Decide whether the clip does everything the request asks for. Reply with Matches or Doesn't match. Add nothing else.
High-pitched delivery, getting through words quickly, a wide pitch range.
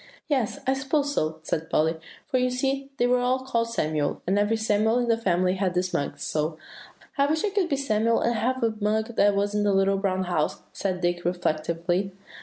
Matches